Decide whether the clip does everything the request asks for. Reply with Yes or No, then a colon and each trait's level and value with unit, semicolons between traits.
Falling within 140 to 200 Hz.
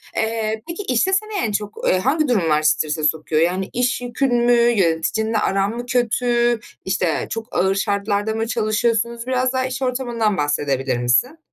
No: high, 225 Hz